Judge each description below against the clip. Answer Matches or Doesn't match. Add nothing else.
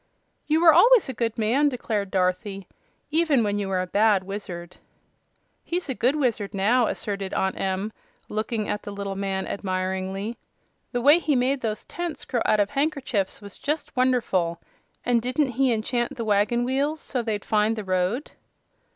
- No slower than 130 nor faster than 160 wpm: Doesn't match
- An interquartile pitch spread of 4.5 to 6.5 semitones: Matches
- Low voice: Doesn't match